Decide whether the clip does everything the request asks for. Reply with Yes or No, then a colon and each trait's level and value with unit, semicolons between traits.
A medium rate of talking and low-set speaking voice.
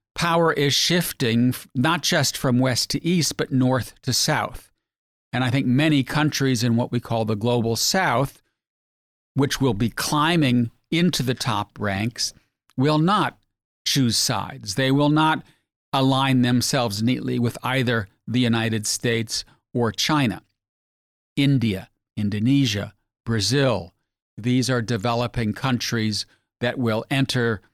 No: slow, 130 wpm; low, 125 Hz